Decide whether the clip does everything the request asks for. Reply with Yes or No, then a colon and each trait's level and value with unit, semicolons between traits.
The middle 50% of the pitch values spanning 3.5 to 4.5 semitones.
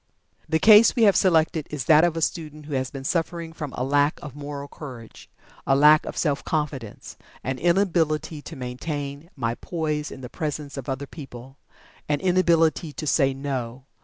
No: average, 3.0 semitones